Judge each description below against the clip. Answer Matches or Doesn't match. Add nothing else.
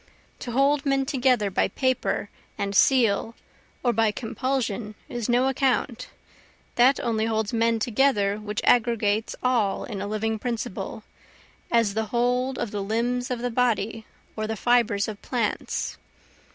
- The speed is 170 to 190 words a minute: Doesn't match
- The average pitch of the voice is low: Doesn't match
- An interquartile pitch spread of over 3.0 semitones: Doesn't match